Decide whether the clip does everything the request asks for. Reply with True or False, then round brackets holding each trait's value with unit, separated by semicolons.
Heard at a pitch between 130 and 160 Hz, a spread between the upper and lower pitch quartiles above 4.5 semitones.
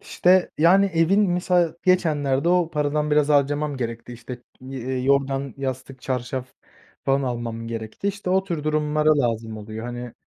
True (140 Hz; 4.9 semitones)